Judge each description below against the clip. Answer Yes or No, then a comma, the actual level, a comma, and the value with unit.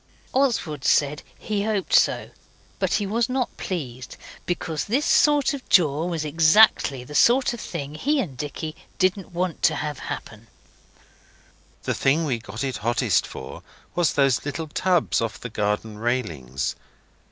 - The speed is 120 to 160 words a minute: Yes, average, 150 wpm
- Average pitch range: No, wide, 7.6 semitones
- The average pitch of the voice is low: No, medium, 155 Hz